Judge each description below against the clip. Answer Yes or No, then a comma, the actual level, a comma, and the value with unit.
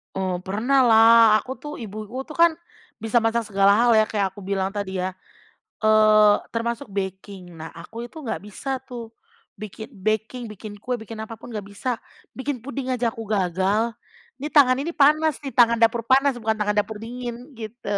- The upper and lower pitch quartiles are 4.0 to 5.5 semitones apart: No, average, 3.4 semitones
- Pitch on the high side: Yes, high, 225 Hz